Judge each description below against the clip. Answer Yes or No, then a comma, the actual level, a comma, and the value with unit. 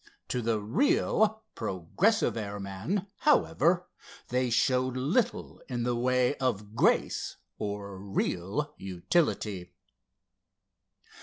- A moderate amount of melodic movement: No, wide, 6.8 semitones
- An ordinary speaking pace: No, slow, 90 wpm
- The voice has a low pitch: Yes, low, 120 Hz